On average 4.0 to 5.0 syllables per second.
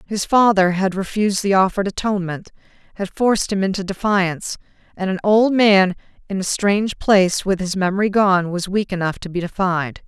No: 5.5 syllables/s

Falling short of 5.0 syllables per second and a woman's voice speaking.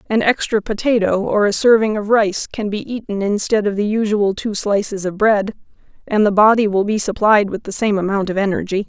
No: 5.4 syllables/s; female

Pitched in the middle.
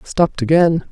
Yes: medium, 155 Hz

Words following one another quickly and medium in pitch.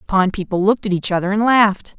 No: fast, 270 wpm; high, 200 Hz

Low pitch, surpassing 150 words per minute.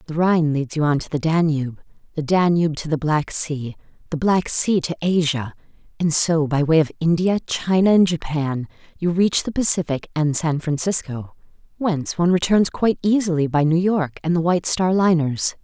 No: medium, 165 Hz; average, 185 wpm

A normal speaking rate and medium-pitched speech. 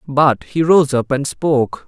Yes: average, 190 wpm; medium, 145 Hz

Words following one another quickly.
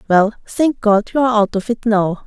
Yes: fast, 210 wpm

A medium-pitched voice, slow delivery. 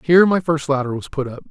No: medium, 150 Hz; fast, 280 wpm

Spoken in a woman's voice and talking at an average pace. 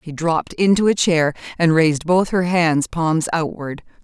Yes: female; average, 180 wpm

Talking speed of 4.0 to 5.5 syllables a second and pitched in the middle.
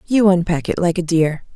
Yes: 5.3 syllables/s; medium, 175 Hz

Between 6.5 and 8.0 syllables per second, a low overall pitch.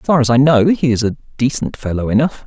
Yes: 6.7 syllables/s; low, 130 Hz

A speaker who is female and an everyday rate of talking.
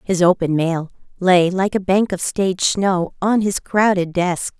Yes: female; average, 185 wpm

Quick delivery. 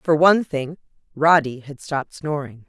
No: average, 155 wpm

